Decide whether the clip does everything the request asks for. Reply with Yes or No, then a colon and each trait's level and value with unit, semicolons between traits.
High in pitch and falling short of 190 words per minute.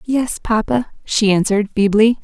Yes: high, 220 Hz; slow, 135 wpm